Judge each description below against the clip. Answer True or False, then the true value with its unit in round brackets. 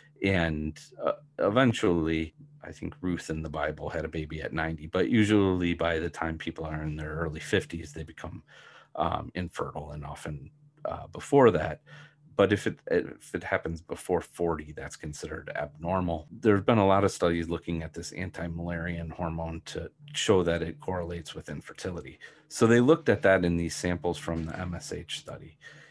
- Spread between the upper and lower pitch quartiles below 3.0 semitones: True (2.6 semitones)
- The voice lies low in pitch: True (85 Hz)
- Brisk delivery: False (175 wpm)